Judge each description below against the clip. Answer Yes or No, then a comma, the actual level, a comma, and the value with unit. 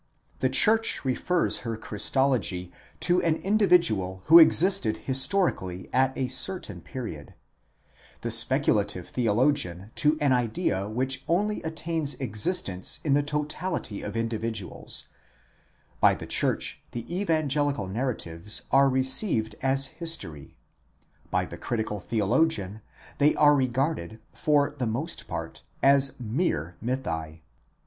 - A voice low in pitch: Yes, low, 130 Hz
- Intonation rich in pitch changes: Yes, wide, 6.1 semitones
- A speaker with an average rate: No, slow, 120 wpm